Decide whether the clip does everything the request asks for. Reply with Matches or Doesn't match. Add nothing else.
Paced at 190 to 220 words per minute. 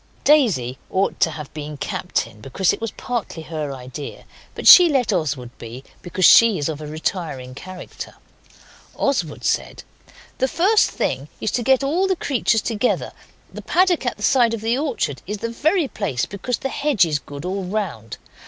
Doesn't match